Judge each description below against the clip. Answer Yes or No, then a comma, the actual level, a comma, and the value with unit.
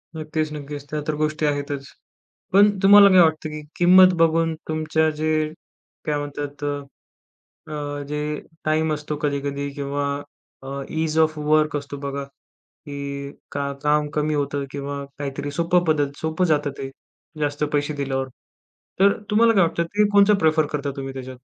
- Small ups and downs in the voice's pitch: Yes, narrow, 1.9 semitones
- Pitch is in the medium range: Yes, medium, 150 Hz